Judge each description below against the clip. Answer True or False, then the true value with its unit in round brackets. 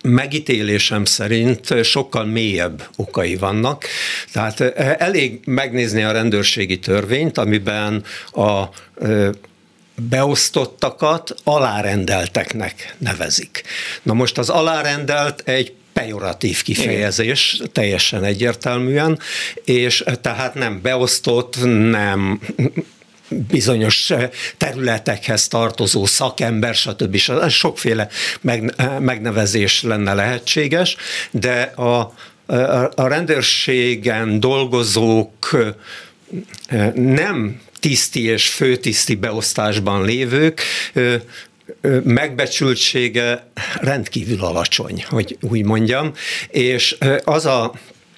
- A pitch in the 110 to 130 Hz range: True (120 Hz)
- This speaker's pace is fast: False (75 wpm)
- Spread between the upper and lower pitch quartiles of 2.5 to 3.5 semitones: True (3.2 semitones)